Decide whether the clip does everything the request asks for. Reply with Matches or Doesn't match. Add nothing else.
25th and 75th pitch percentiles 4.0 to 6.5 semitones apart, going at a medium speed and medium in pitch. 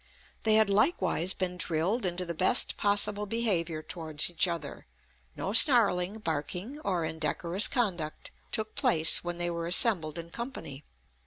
Matches